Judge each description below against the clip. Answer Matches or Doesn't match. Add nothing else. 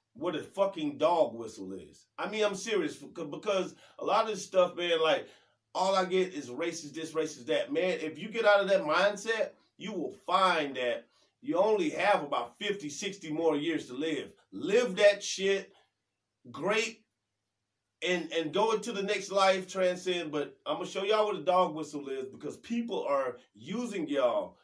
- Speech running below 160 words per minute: Doesn't match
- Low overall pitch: Doesn't match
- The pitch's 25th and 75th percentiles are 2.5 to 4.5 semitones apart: Doesn't match